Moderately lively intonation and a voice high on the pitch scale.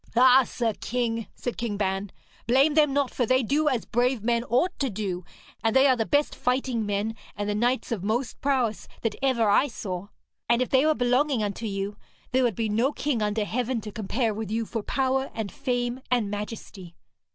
Yes: average, 3.6 semitones; high, 235 Hz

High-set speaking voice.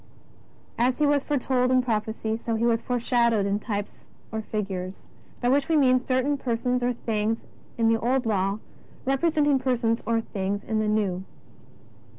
Yes: high, 235 Hz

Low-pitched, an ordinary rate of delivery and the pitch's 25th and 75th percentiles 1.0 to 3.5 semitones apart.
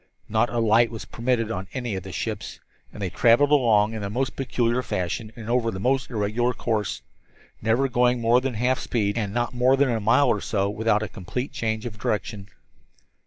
No: low, 115 Hz; fast, 210 wpm; average, 2.8 semitones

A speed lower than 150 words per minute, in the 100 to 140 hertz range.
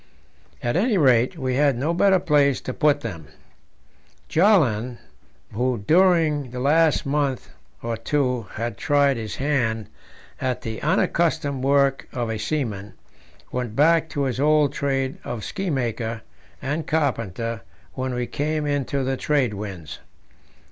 Yes: average, 140 wpm; low, 135 Hz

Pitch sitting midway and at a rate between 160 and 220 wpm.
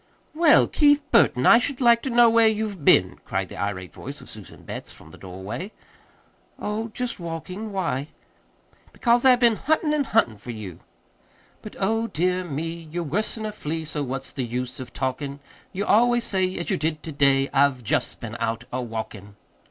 Yes: medium, 170 Hz; average, 185 wpm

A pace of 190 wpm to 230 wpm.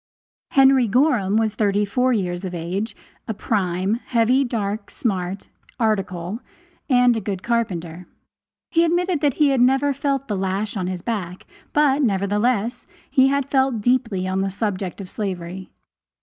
No: average, 150 wpm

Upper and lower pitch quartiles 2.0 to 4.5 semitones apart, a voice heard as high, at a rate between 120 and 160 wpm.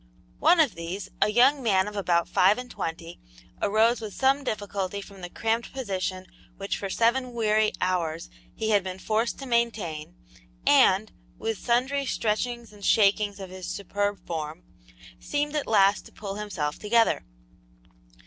Yes: average, 3.9 semitones; high, 210 Hz; average, 155 wpm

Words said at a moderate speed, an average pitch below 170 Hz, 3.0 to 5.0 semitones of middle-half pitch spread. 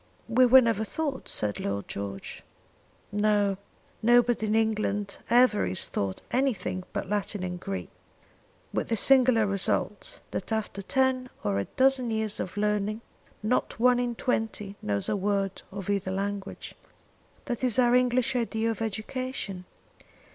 No: average, 145 wpm; high, 215 Hz; average, 3.7 semitones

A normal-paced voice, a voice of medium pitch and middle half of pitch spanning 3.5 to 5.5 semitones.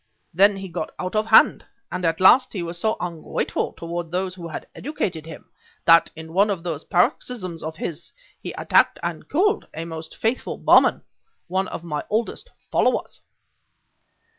Yes: average, 165 wpm; medium, 180 Hz; average, 4.0 semitones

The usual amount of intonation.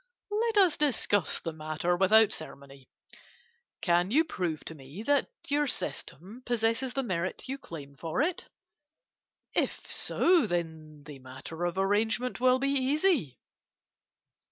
No: wide, 9.0 semitones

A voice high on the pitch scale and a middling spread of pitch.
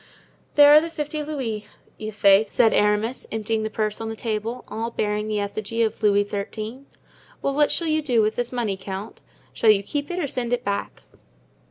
Yes: high, 220 Hz; average, 3.5 semitones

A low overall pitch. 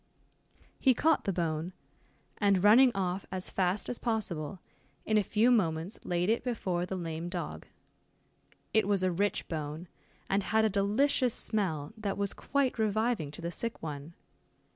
No: high, 195 Hz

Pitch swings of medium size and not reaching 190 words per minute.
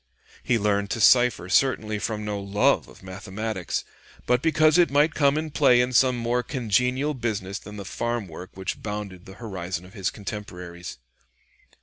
Yes: average, 4.4 semitones; average, 170 wpm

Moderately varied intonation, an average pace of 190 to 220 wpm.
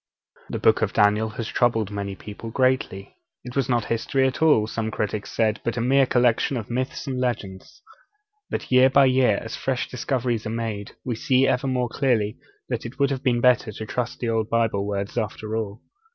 Yes: average, 3.0 semitones; average, 200 wpm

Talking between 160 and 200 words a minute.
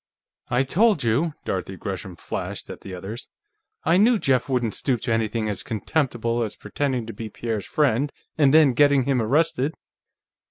Yes: average, 165 wpm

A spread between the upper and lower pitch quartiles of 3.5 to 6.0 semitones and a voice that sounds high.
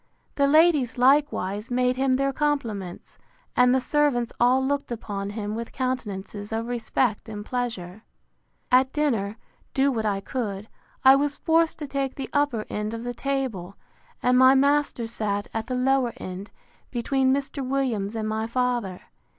Yes: average, 4.0 semitones; high, 245 Hz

